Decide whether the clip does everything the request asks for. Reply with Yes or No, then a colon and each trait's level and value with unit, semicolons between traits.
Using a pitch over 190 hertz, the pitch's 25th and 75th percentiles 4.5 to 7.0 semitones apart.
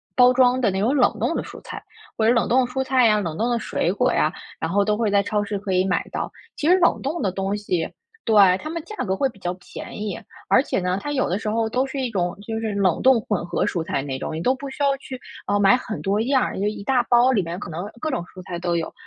Yes: high, 215 Hz; average, 5.3 semitones